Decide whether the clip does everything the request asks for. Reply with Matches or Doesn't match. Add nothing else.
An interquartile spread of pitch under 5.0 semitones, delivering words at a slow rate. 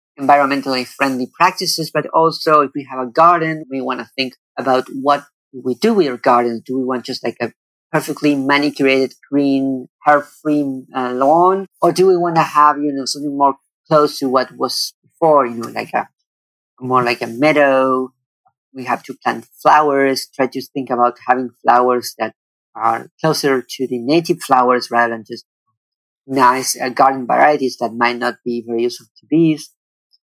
Doesn't match